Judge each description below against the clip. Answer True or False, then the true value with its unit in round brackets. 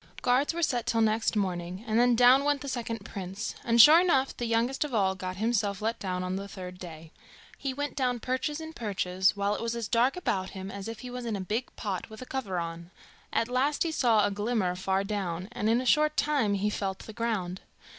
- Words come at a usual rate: False (235 wpm)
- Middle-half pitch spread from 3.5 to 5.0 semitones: True (4.6 semitones)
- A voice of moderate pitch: False (220 Hz)